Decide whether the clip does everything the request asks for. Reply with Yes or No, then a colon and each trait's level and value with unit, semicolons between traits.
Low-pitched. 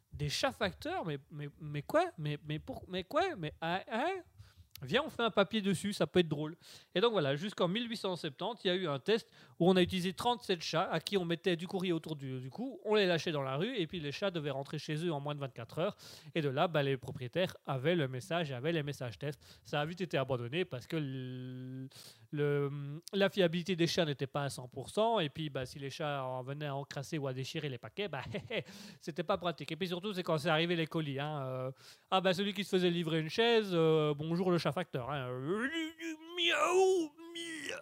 No: medium, 165 Hz